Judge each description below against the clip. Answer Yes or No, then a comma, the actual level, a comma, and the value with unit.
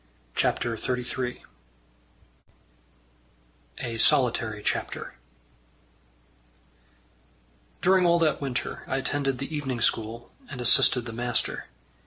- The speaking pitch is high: No, low, 125 Hz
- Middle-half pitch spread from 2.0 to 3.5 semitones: Yes, average, 2.8 semitones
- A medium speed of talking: No, slow, 90 wpm